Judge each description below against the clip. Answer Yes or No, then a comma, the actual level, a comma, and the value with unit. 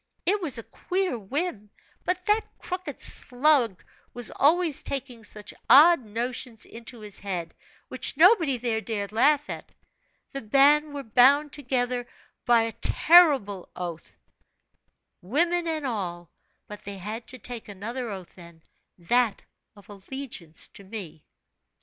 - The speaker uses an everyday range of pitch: No, wide, 6.0 semitones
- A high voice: Yes, high, 245 Hz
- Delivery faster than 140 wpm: No, slow, 135 wpm